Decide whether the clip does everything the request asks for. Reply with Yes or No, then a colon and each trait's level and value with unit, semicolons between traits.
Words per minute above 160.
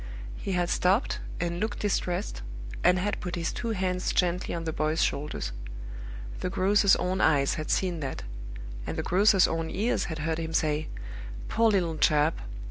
Yes: average, 170 wpm